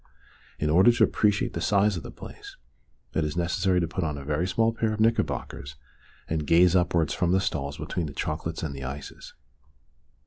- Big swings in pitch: No, average, 4.0 semitones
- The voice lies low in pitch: Yes, very low, 85 Hz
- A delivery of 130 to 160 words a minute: No, average, 195 wpm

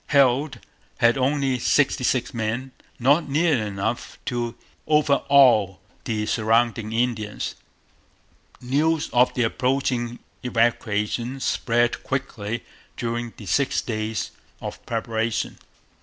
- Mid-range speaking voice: No, low, 120 Hz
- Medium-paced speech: No, slow, 100 wpm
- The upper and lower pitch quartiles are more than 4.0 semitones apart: No, average, 3.1 semitones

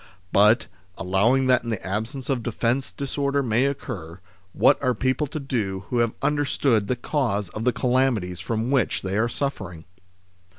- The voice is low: Yes, low, 120 Hz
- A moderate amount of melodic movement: Yes, average, 4.4 semitones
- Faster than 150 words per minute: Yes, average, 165 wpm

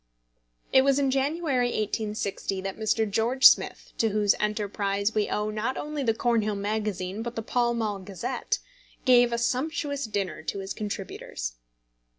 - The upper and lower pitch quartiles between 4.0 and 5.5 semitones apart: No, average, 3.4 semitones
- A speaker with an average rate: Yes, average, 155 wpm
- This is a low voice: No, high, 220 Hz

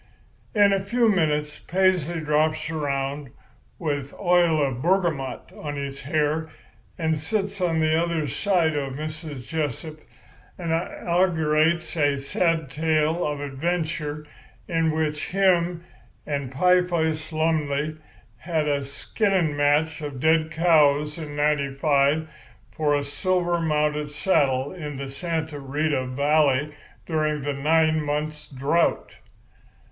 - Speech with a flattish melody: Yes, narrow, 2.3 semitones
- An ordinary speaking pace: No, slow, 120 wpm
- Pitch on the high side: No, medium, 155 Hz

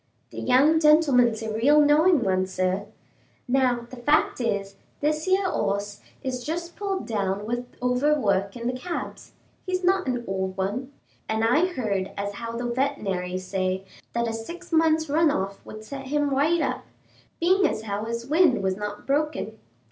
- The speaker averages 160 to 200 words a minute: Yes, average, 170 wpm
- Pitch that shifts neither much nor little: No, wide, 6.9 semitones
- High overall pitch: Yes, high, 245 Hz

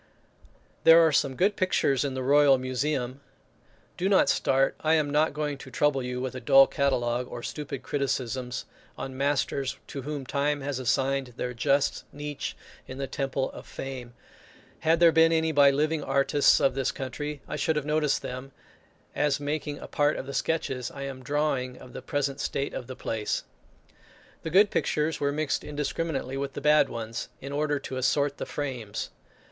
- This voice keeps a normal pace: Yes, average, 180 wpm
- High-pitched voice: No, medium, 140 Hz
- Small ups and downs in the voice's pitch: Yes, narrow, 2.2 semitones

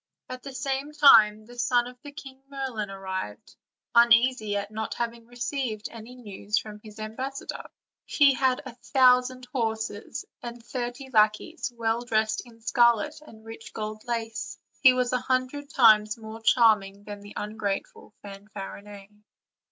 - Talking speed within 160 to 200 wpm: No, average, 150 wpm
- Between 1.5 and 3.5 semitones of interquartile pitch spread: Yes, average, 3.0 semitones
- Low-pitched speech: No, high, 230 Hz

